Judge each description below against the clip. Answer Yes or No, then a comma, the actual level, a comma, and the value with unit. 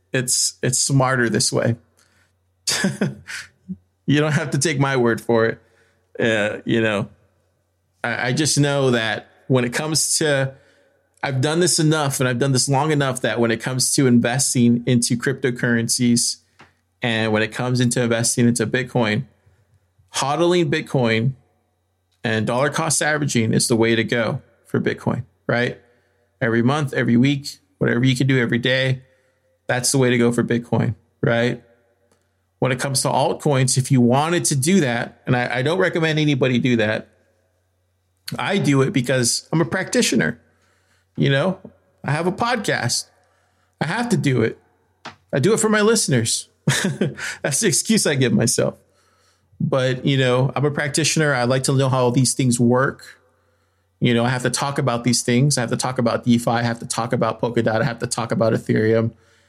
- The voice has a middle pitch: No, low, 125 Hz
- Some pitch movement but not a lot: Yes, average, 3.6 semitones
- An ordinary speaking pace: Yes, average, 175 wpm